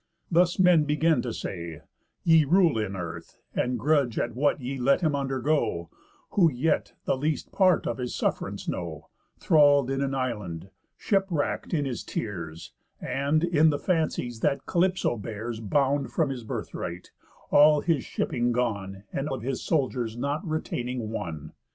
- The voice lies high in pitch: No, low, 135 Hz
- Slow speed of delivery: No, average, 155 wpm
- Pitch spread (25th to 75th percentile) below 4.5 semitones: No, wide, 5.4 semitones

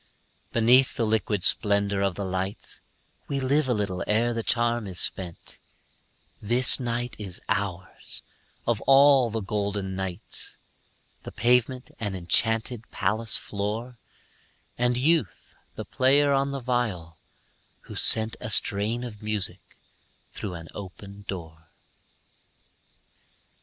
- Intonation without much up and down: No, average, 3.8 semitones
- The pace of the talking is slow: Yes, slow, 120 wpm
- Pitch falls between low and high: No, low, 110 Hz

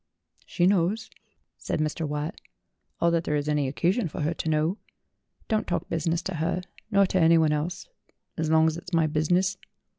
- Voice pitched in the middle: Yes, medium, 165 Hz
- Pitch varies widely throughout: No, average, 2.9 semitones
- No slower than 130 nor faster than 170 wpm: No, average, 180 wpm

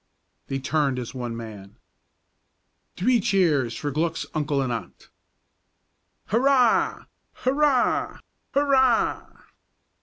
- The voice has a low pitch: No, medium, 155 Hz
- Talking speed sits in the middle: No, slow, 90 wpm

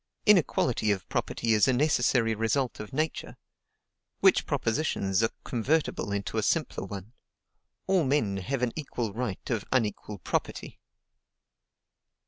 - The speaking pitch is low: Yes, low, 115 Hz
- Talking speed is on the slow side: Yes, slow, 125 wpm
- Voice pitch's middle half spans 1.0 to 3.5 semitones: No, average, 4.7 semitones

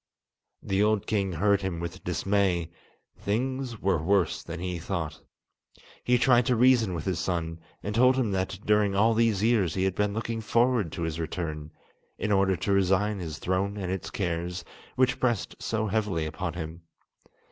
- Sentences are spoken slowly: No, average, 175 wpm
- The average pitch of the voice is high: No, very low, 95 Hz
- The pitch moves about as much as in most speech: Yes, average, 4.1 semitones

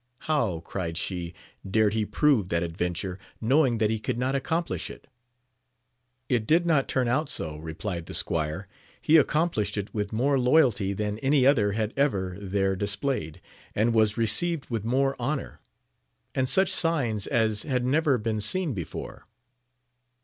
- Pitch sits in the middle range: No, low, 115 Hz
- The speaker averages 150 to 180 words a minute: Yes, average, 155 wpm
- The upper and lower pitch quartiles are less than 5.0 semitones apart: No, wide, 5.6 semitones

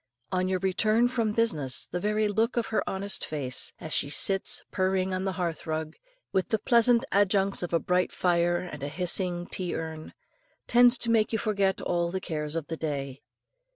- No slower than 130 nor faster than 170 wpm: No, average, 190 wpm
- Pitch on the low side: No, medium, 185 Hz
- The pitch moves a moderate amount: Yes, average, 4.4 semitones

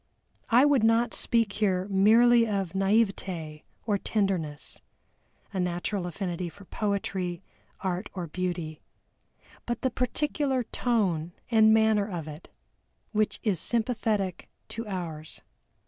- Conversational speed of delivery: No, slow, 115 wpm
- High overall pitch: Yes, high, 200 Hz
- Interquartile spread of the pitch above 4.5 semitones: No, average, 4.2 semitones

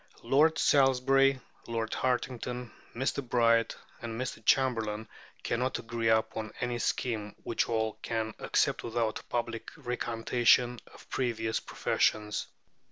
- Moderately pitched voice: No, low, 120 Hz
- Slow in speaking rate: Yes, slow, 115 wpm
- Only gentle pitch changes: Yes, narrow, 2.0 semitones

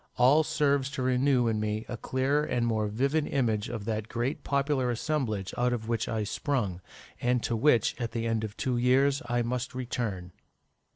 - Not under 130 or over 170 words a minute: No, average, 185 wpm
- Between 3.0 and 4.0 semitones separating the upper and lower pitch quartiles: Yes, average, 3.3 semitones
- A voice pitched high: No, low, 120 Hz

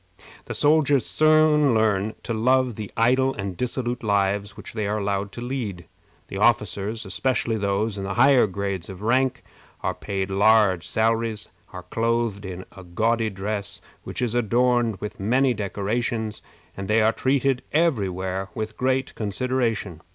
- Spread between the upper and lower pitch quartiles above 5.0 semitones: No, average, 3.7 semitones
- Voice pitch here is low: Yes, low, 110 Hz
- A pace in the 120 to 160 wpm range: Yes, average, 155 wpm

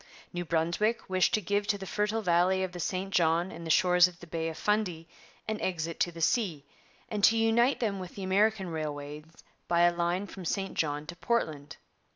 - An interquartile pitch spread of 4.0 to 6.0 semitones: No, average, 3.6 semitones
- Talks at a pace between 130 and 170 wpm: No, fast, 205 wpm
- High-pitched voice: No, medium, 180 Hz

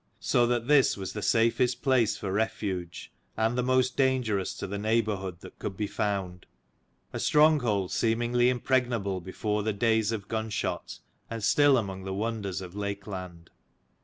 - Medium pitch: No, low, 110 Hz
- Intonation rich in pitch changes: No, average, 3.8 semitones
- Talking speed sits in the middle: Yes, average, 160 wpm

